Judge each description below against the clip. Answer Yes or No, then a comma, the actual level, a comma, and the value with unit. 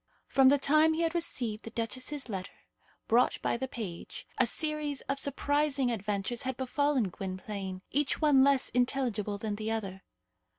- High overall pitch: Yes, very high, 250 Hz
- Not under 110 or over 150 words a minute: No, average, 160 wpm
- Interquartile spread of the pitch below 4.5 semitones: No, average, 5.3 semitones